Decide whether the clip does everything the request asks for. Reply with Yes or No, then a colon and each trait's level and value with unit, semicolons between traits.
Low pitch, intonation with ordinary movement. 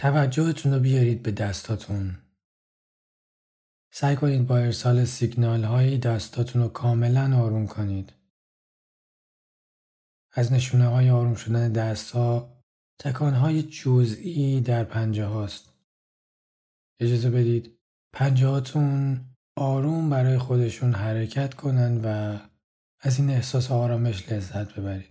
Yes: low, 120 Hz; average, 3.0 semitones